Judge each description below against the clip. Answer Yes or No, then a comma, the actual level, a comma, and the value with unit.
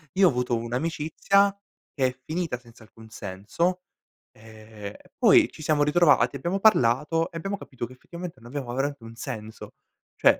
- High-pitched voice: No, low, 130 Hz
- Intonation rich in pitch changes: Yes, wide, 6.2 semitones